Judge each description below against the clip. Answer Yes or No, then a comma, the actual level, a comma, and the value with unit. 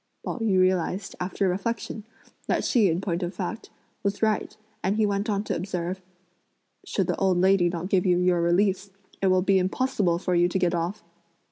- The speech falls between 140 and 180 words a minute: No, average, 195 wpm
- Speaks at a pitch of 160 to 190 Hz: Yes, medium, 185 Hz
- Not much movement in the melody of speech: Yes, narrow, 2.2 semitones